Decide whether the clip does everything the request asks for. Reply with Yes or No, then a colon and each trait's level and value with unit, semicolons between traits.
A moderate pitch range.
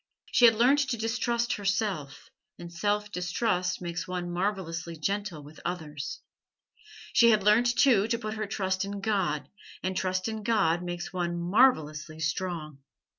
Yes: average, 4.0 semitones